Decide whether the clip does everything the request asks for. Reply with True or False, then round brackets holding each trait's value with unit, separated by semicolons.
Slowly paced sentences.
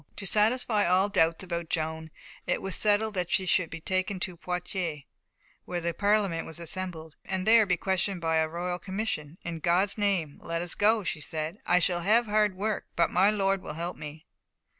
False (195 wpm)